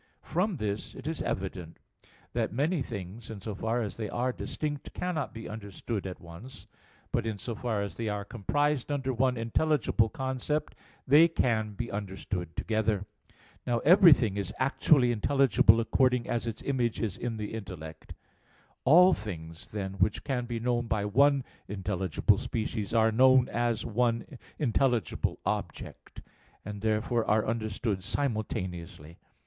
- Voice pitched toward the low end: Yes, low, 115 Hz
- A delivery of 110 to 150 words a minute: Yes, average, 145 wpm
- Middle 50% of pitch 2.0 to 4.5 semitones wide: Yes, average, 4.1 semitones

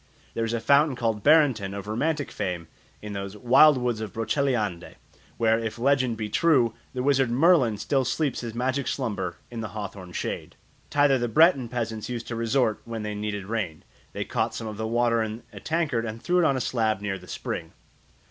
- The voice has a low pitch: Yes, low, 115 Hz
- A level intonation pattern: No, average, 3.8 semitones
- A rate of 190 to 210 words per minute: Yes, average, 200 wpm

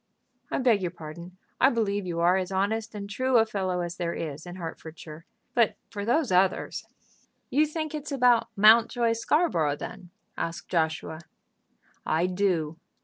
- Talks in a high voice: Yes, high, 195 Hz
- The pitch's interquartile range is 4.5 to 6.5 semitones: Yes, average, 5.3 semitones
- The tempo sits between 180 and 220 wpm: No, average, 160 wpm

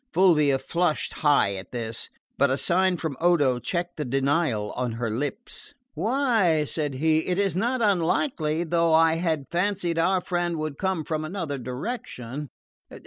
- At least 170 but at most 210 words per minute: No, average, 155 wpm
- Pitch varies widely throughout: No, average, 4.3 semitones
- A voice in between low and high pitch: Yes, medium, 160 Hz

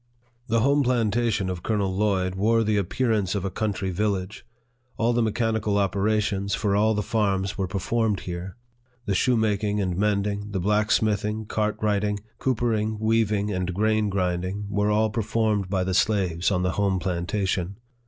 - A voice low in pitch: Yes, low, 105 Hz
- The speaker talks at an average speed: Yes, average, 155 wpm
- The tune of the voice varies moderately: No, narrow, 2.2 semitones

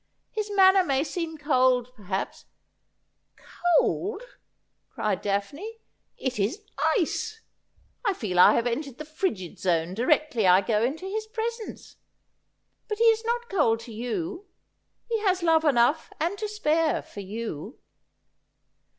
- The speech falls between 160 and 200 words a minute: No, average, 150 wpm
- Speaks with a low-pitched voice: No, very high, 305 Hz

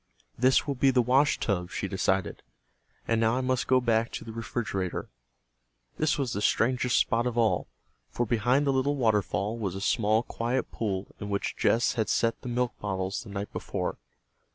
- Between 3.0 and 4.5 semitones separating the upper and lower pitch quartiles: Yes, average, 3.5 semitones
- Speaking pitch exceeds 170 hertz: No, low, 115 Hz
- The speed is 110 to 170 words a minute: No, average, 180 wpm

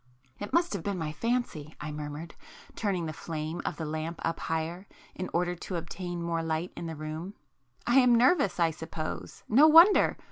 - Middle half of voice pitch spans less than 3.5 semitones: No, average, 4.2 semitones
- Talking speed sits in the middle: Yes, average, 175 wpm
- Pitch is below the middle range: No, medium, 170 Hz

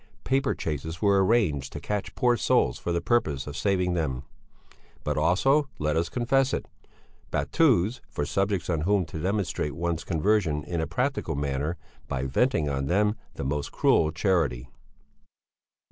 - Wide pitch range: Yes, wide, 5.8 semitones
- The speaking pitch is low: Yes, very low, 85 Hz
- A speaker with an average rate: Yes, average, 155 wpm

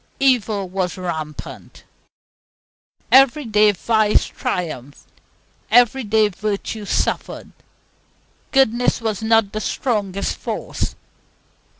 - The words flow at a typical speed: No, slow, 85 wpm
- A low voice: No, high, 215 Hz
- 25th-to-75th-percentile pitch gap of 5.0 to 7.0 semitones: No, average, 3.2 semitones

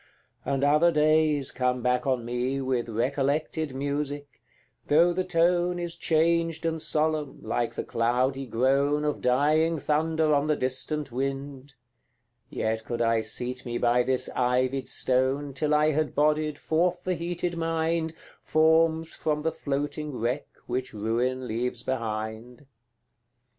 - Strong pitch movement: No, average, 3.8 semitones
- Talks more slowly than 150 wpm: Yes, average, 140 wpm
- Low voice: No, medium, 145 Hz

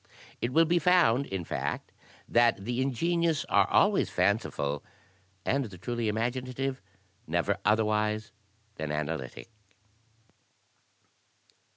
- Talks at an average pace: No, slow, 100 wpm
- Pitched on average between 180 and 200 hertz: No, low, 120 Hz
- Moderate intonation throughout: Yes, average, 4.4 semitones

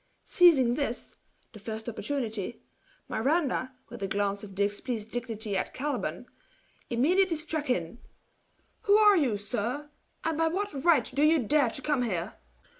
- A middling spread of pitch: No, wide, 6.0 semitones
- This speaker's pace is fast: No, average, 145 wpm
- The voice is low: No, very high, 255 Hz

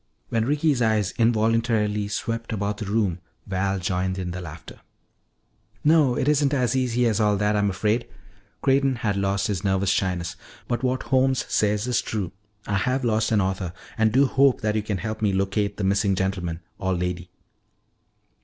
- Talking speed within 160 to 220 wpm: Yes, average, 175 wpm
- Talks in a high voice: No, low, 105 Hz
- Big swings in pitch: No, average, 3.7 semitones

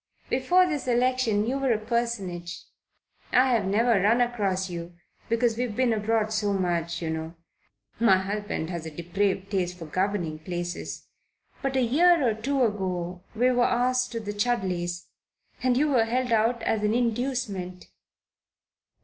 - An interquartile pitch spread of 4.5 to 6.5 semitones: Yes, average, 5.1 semitones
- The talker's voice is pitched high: Yes, high, 215 Hz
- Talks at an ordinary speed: Yes, average, 155 wpm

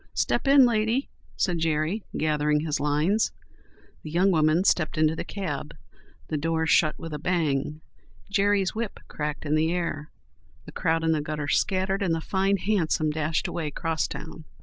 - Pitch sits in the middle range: Yes, medium, 160 Hz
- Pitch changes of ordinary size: Yes, average, 3.8 semitones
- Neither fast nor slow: Yes, average, 165 wpm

